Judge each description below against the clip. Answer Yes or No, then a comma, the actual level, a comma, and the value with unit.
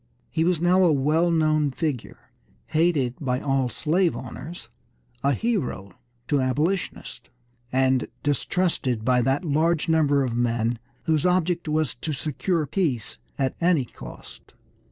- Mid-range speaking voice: Yes, medium, 150 Hz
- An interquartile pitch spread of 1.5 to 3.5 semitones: No, average, 4.4 semitones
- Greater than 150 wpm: No, slow, 135 wpm